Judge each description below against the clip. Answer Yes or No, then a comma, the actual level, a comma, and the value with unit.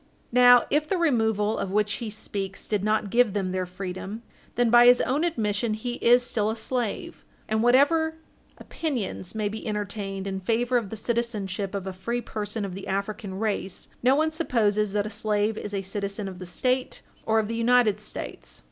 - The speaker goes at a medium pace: Yes, average, 190 wpm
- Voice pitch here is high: Yes, high, 215 Hz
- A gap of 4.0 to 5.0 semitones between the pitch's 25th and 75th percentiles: No, average, 3.3 semitones